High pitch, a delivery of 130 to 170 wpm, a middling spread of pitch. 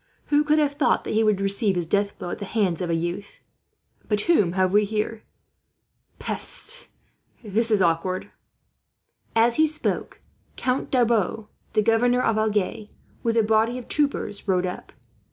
Yes: high, 215 Hz; average, 165 wpm; average, 3.3 semitones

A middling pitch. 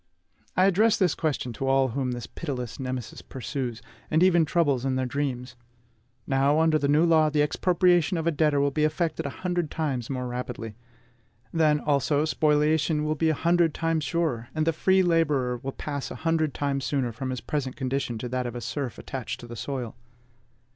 Yes: medium, 145 Hz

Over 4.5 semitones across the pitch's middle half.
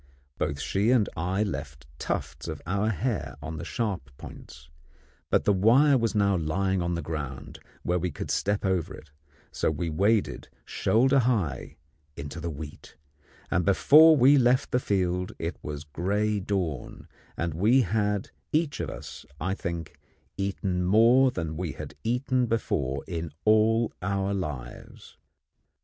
Yes: wide, 5.5 semitones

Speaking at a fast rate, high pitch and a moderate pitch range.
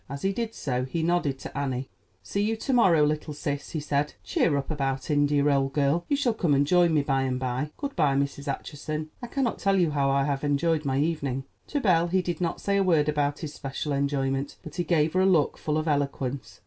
No: fast, 235 wpm; medium, 150 Hz; average, 3.6 semitones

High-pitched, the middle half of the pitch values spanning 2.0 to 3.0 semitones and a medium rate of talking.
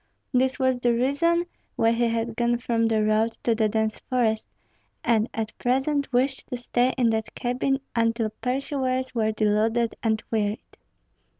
Yes: high, 235 Hz; narrow, 2.5 semitones; average, 160 wpm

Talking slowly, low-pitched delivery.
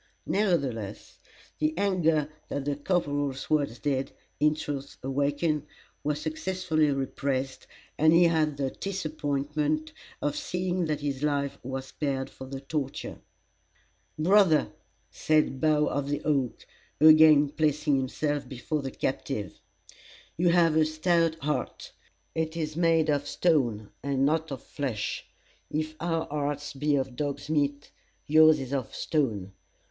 No: slow, 130 wpm; medium, 150 Hz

